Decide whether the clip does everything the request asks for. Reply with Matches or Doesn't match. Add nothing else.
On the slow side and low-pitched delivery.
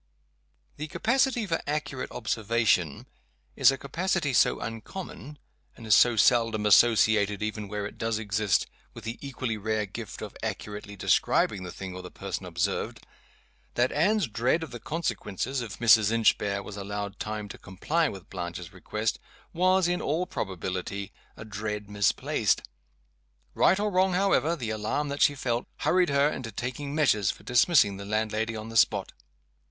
Doesn't match